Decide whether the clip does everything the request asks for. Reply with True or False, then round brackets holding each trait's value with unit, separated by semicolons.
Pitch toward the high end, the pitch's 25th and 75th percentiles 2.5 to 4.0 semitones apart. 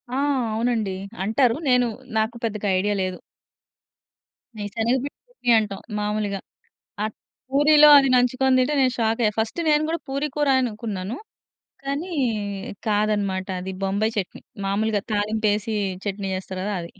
True (220 Hz; 3.7 semitones)